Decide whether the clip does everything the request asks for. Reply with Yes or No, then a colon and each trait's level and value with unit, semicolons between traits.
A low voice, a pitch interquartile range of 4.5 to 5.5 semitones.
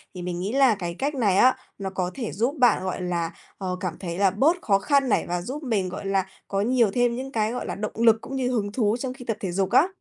No: high, 215 Hz; average, 5.0 semitones